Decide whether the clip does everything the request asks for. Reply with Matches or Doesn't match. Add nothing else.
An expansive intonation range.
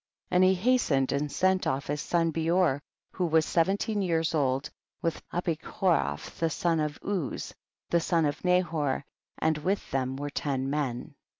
Doesn't match